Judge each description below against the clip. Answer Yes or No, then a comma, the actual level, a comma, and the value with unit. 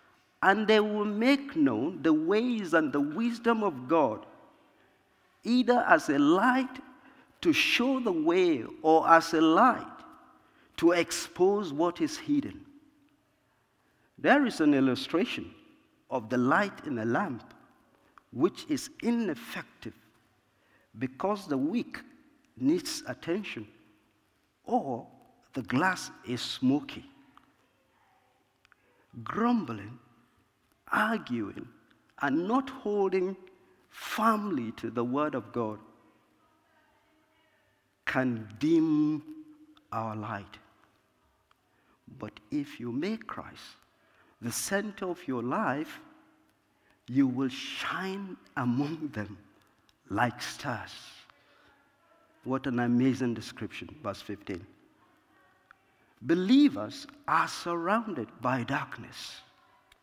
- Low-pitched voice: No, high, 210 Hz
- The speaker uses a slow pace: Yes, slow, 95 wpm